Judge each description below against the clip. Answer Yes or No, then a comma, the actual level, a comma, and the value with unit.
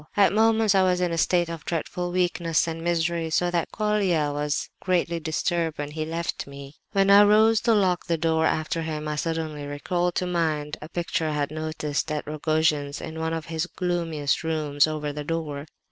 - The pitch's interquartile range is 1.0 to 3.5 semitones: Yes, narrow, 2.5 semitones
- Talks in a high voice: No, medium, 165 Hz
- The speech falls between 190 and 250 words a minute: Yes, average, 195 wpm